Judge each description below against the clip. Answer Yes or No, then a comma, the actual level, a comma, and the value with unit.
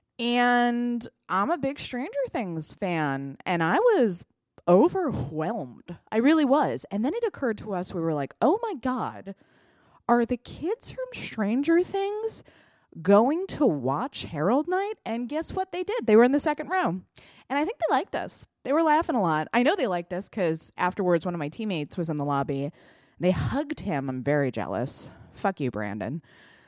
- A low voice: No, high, 220 Hz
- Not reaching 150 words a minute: No, average, 185 wpm